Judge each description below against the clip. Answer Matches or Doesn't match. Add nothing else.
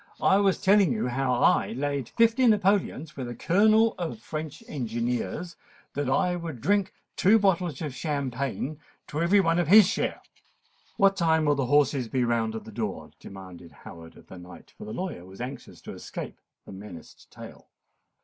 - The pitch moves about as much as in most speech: Doesn't match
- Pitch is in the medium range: Matches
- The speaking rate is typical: Matches